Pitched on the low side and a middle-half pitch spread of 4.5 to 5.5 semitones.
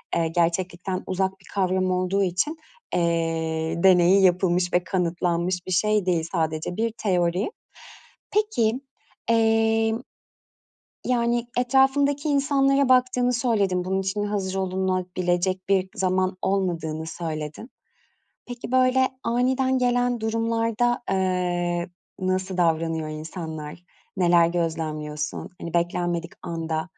No: medium, 185 Hz; average, 4.8 semitones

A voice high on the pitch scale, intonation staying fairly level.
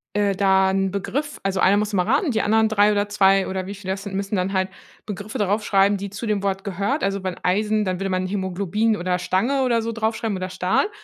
Yes: high, 200 Hz; narrow, 1.9 semitones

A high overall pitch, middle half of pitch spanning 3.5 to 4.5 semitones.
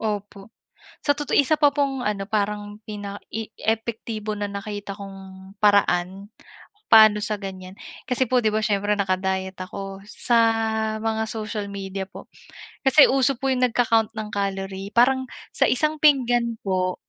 No: high, 210 Hz; average, 3.0 semitones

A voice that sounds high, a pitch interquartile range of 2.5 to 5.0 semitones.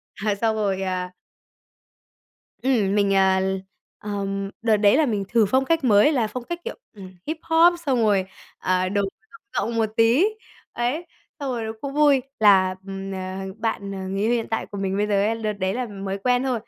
Yes: high, 210 Hz; average, 4.3 semitones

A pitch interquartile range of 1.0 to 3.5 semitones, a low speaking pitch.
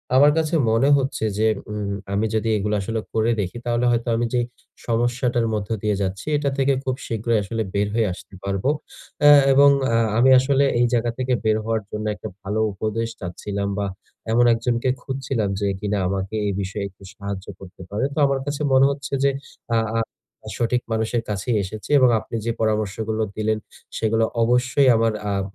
Yes: average, 3.1 semitones; low, 115 Hz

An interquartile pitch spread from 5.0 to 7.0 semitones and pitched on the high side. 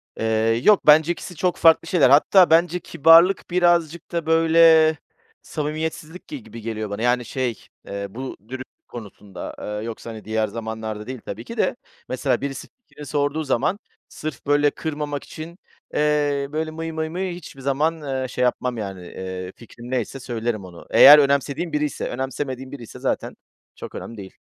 No: wide, 5.5 semitones; medium, 140 Hz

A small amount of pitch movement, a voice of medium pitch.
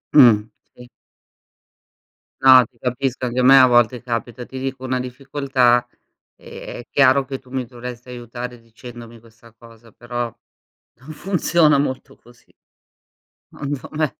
No: narrow, 1.8 semitones; low, 125 Hz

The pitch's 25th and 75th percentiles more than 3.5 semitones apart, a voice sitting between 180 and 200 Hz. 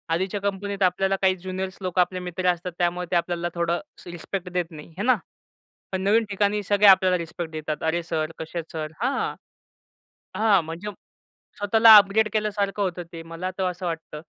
No: average, 2.8 semitones; medium, 185 Hz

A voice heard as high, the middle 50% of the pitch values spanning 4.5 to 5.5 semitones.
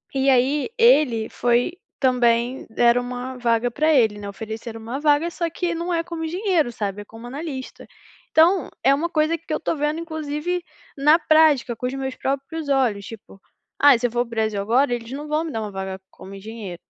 Yes: very high, 265 Hz; average, 5.2 semitones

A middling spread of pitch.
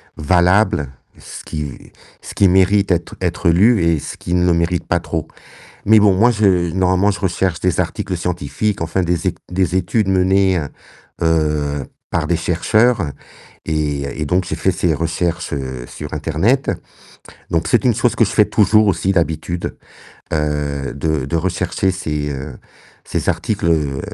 Yes: average, 3.6 semitones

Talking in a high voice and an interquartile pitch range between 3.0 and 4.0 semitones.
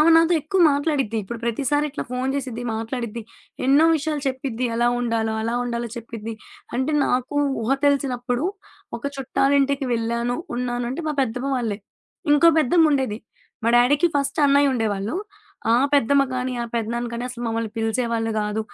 Yes: very high, 250 Hz; average, 3.3 semitones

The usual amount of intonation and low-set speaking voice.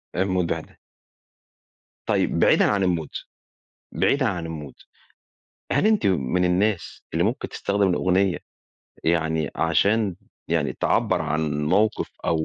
Yes: average, 3.7 semitones; very low, 90 Hz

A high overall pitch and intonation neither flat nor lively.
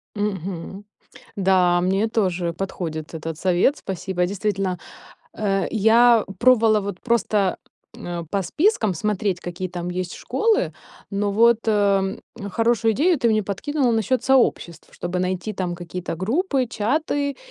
Yes: high, 200 Hz; average, 4.0 semitones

